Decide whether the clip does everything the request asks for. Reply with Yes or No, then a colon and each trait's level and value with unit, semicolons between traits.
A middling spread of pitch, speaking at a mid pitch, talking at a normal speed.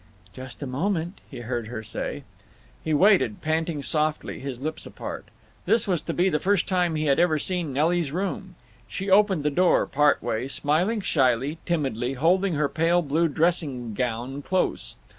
Yes: average, 4.7 semitones; medium, 155 Hz; average, 170 wpm